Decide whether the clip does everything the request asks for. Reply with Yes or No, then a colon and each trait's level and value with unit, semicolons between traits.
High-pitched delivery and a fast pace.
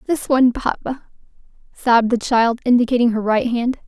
No: high, 240 Hz; average, 155 wpm